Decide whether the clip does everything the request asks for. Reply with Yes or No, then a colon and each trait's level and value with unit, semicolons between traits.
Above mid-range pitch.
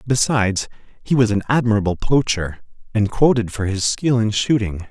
No: low, 110 Hz